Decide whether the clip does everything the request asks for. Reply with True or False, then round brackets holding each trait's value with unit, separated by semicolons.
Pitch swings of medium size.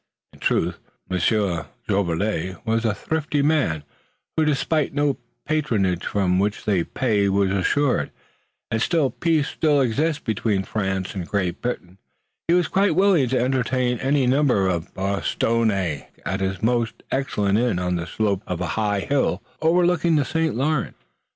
False (7.0 semitones)